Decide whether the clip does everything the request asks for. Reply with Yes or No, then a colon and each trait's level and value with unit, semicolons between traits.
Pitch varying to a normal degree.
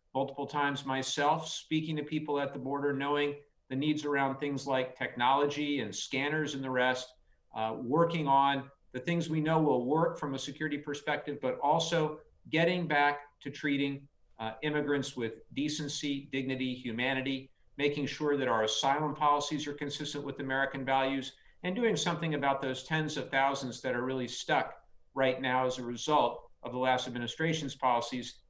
No: narrow, 2.1 semitones